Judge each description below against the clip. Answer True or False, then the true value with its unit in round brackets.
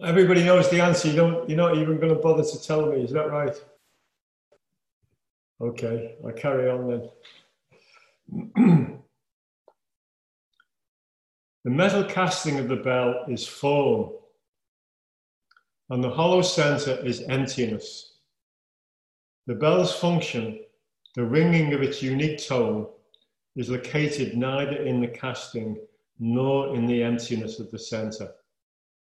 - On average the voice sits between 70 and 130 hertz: False (140 Hz)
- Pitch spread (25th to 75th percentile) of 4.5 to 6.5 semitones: True (5.5 semitones)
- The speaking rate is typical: False (120 wpm)